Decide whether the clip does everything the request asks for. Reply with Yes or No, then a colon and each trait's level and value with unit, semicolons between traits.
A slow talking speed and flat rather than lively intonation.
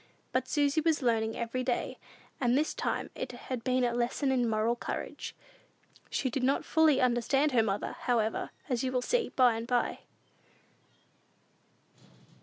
No: average, 155 wpm; narrow, 2.3 semitones